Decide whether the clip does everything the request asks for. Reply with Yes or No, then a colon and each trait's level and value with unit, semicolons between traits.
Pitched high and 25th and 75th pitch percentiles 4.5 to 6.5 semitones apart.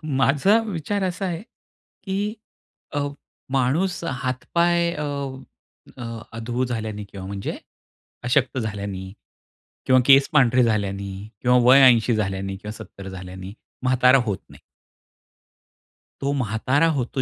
No: low, 125 Hz; wide, 5.4 semitones